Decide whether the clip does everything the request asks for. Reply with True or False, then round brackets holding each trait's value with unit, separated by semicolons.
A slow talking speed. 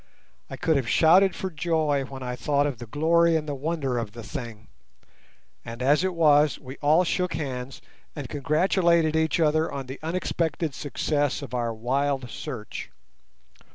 False (165 wpm)